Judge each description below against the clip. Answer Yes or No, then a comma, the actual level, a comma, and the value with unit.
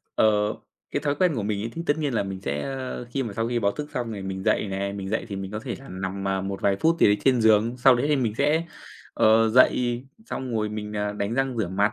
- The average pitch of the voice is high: No, low, 110 Hz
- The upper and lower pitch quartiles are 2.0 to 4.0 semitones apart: No, average, 4.6 semitones